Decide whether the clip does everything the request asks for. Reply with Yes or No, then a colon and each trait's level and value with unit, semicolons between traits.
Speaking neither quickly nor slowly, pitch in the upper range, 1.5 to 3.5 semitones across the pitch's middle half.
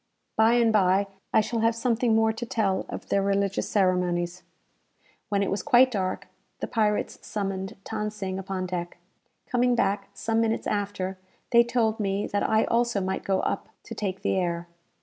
Yes: average, 180 wpm; high, 205 Hz; average, 2.9 semitones